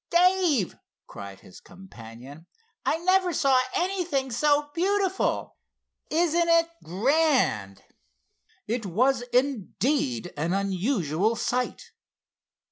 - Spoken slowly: Yes, slow, 90 wpm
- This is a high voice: Yes, very high, 255 Hz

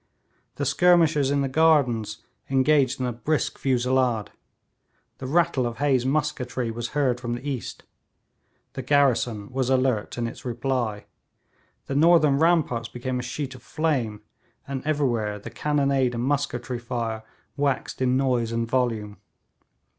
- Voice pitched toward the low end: Yes, low, 130 Hz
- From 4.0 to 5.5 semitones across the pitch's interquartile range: No, average, 3.1 semitones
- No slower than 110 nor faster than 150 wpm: Yes, average, 140 wpm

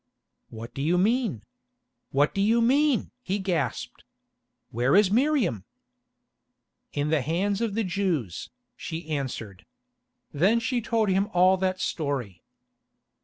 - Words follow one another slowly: Yes, slow, 125 wpm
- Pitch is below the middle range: No, medium, 185 Hz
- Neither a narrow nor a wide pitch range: No, wide, 7.1 semitones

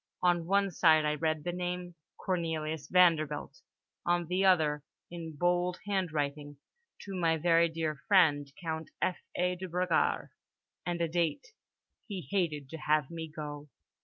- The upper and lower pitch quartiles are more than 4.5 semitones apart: No, average, 2.7 semitones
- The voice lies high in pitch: No, medium, 165 Hz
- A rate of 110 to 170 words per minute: Yes, slow, 135 wpm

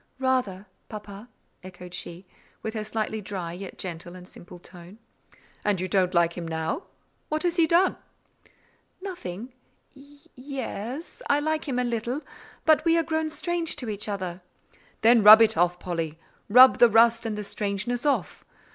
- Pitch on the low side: No, high, 220 Hz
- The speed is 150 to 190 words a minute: Yes, average, 160 wpm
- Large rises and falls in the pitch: Yes, wide, 7.1 semitones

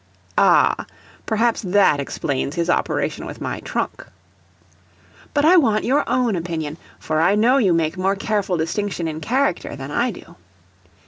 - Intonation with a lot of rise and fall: Yes, wide, 6.3 semitones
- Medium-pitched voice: No, high, 195 Hz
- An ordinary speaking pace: Yes, average, 150 wpm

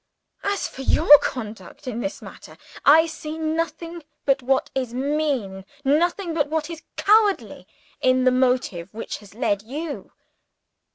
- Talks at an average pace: Yes, average, 150 wpm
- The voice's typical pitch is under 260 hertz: No, very high, 285 Hz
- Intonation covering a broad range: No, average, 4.4 semitones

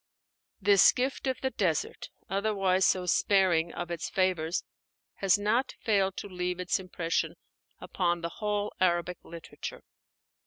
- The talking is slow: Yes, slow, 130 wpm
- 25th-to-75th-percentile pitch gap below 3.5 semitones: Yes, average, 2.8 semitones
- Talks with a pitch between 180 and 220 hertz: Yes, medium, 185 Hz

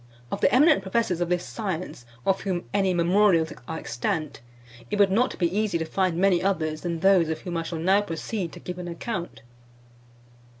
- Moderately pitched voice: Yes, medium, 180 Hz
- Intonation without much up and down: No, average, 3.1 semitones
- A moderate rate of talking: Yes, average, 190 wpm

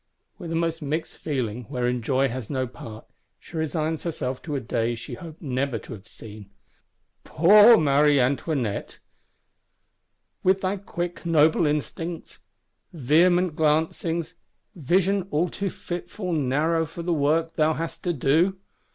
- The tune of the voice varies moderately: Yes, average, 4.4 semitones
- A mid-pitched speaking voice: Yes, medium, 155 Hz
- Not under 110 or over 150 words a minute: Yes, average, 140 wpm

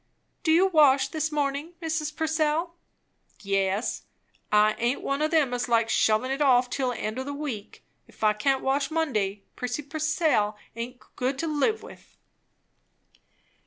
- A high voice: Yes, very high, 275 Hz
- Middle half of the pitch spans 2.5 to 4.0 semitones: No, average, 4.8 semitones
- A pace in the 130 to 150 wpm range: No, average, 160 wpm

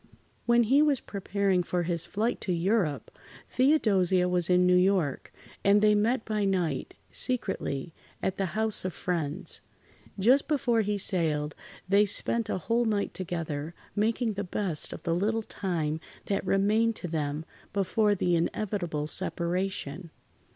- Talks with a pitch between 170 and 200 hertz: Yes, high, 190 Hz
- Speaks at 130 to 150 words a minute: Yes, average, 145 wpm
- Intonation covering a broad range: No, average, 3.8 semitones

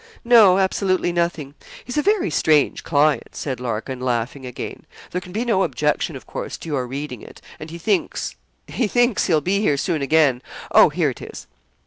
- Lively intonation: Yes, wide, 6.3 semitones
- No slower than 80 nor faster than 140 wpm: No, average, 185 wpm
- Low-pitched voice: No, medium, 165 Hz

